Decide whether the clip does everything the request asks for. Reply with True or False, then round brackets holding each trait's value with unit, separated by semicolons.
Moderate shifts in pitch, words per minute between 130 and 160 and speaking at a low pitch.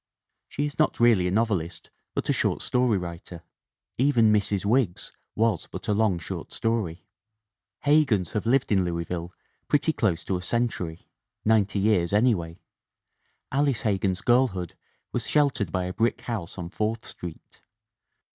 True (4.9 semitones; 155 wpm; 105 Hz)